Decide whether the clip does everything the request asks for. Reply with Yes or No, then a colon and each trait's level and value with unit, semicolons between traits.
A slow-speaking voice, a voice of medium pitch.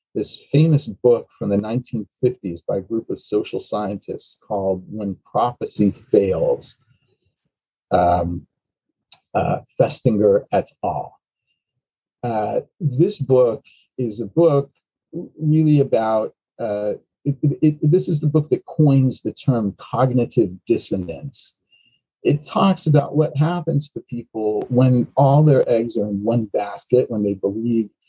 No: slow, 130 wpm; low, 130 Hz